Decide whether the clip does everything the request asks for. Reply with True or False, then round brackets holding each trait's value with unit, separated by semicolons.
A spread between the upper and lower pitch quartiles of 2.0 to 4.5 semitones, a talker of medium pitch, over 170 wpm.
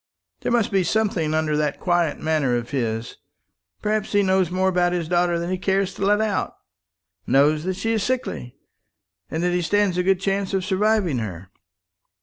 True (4.2 semitones; 180 Hz; 185 wpm)